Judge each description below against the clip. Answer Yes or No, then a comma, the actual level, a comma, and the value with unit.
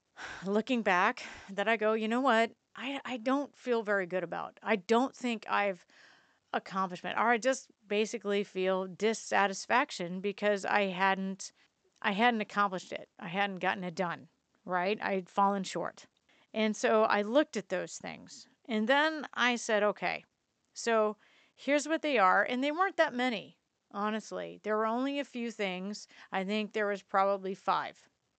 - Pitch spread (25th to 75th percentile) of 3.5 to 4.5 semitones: Yes, average, 3.8 semitones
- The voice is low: No, high, 215 Hz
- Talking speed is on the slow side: No, average, 165 wpm